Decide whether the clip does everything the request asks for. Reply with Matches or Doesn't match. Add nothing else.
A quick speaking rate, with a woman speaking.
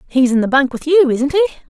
Matches